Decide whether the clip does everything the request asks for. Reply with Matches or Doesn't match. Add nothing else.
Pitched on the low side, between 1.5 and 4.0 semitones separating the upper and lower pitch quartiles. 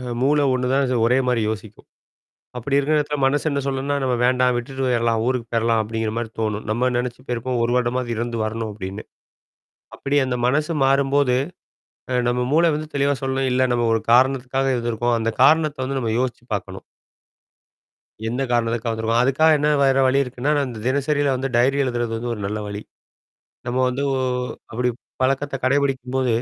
Matches